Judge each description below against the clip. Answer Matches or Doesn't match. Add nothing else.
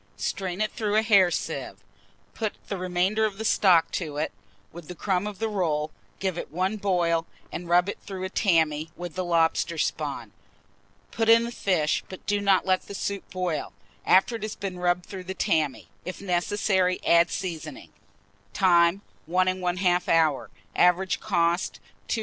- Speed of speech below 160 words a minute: Doesn't match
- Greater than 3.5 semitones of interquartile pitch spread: Doesn't match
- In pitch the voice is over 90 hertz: Matches